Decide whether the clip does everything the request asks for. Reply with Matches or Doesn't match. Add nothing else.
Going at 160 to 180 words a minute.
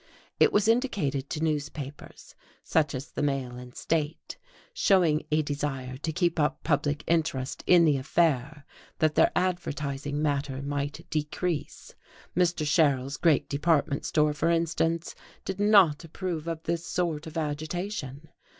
Doesn't match